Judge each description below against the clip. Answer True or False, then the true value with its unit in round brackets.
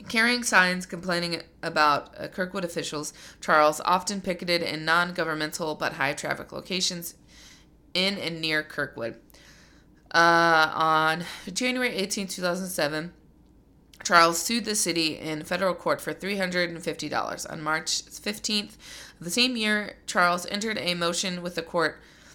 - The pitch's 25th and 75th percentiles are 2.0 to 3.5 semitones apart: True (2.9 semitones)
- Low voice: False (175 Hz)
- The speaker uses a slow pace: True (125 wpm)